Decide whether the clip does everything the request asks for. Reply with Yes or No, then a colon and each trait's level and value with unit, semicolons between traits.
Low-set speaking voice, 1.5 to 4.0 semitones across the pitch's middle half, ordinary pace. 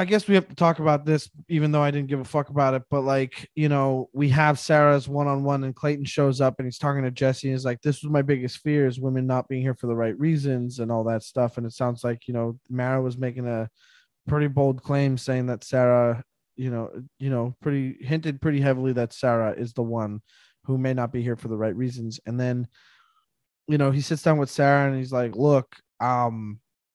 No: low, 130 Hz; average, 2.8 semitones; fast, 240 wpm